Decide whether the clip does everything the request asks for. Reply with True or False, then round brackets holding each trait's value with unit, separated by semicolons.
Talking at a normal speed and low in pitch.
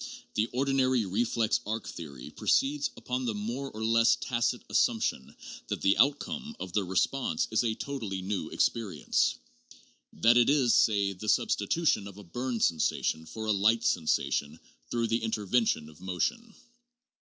True (155 wpm; 110 Hz)